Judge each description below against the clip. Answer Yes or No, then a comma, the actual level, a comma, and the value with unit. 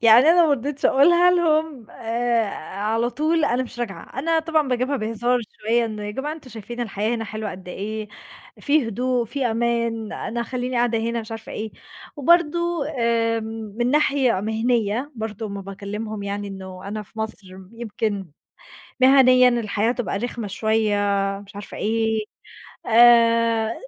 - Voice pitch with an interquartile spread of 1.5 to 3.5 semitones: Yes, average, 2.9 semitones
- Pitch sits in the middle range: No, high, 230 Hz